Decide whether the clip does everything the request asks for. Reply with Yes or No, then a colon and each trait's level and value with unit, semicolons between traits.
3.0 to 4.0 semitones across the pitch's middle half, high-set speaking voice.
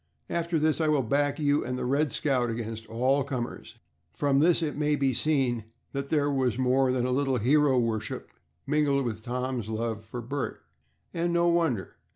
No: average, 3.5 semitones; low, 135 Hz